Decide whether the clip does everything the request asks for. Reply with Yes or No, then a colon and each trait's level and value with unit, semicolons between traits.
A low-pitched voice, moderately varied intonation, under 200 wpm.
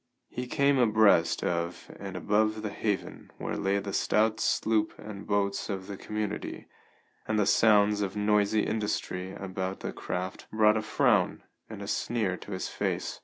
No: low, 105 Hz; narrow, 1.9 semitones; average, 165 wpm